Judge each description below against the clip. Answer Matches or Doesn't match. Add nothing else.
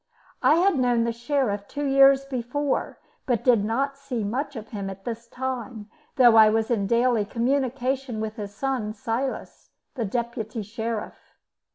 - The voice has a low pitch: Doesn't match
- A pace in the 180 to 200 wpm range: Doesn't match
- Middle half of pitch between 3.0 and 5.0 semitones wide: Matches